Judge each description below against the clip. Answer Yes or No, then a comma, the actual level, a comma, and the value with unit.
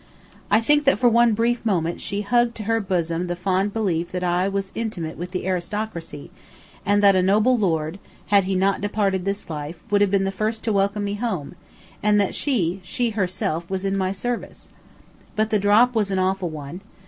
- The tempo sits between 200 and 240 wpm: Yes, fast, 205 wpm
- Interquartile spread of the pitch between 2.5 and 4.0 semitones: Yes, average, 3.0 semitones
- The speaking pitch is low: No, high, 195 Hz